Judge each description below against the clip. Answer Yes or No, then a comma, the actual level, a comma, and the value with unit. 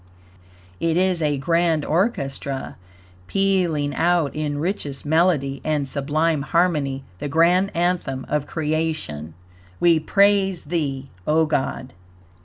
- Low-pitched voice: No, medium, 155 Hz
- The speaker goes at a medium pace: No, slow, 110 wpm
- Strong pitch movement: No, average, 3.5 semitones